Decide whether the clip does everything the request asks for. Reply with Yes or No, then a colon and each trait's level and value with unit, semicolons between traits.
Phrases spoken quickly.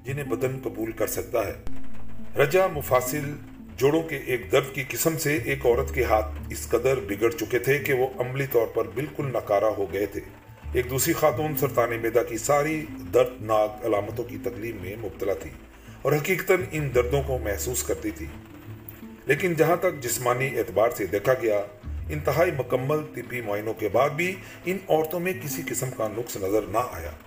No: average, 180 wpm